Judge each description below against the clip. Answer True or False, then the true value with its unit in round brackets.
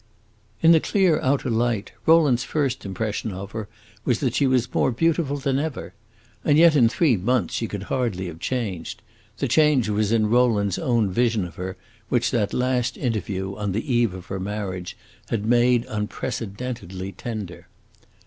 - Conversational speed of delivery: True (170 wpm)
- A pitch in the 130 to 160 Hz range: False (115 Hz)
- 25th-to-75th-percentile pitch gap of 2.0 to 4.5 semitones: True (4.2 semitones)